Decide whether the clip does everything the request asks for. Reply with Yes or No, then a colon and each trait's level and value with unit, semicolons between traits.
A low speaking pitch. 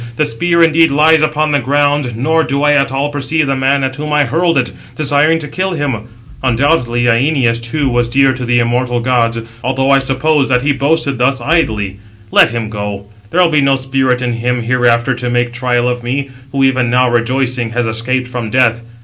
Yes: low, 130 Hz